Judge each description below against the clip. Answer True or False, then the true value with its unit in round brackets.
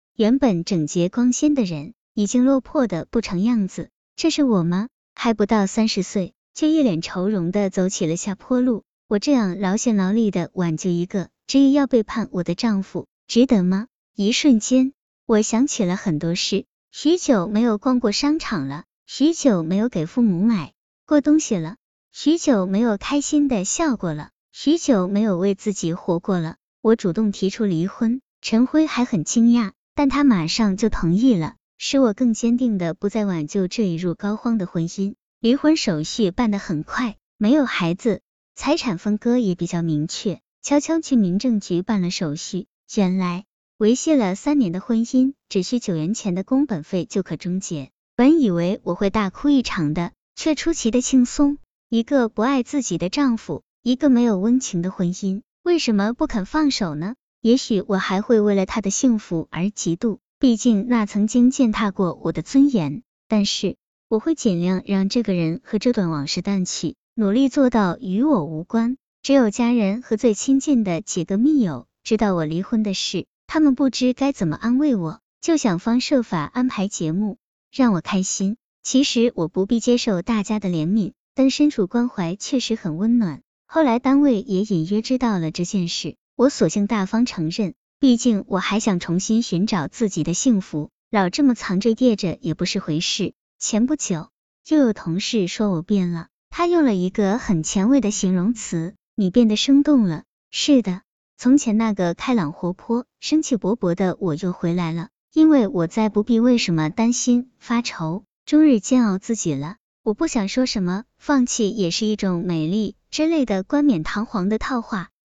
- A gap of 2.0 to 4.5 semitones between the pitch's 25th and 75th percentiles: False (5.2 semitones)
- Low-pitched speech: False (215 Hz)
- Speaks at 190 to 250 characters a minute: False (260 characters per minute)